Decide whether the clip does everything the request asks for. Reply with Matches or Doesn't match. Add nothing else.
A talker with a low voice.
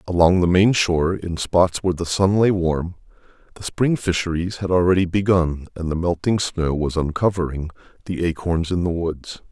Matches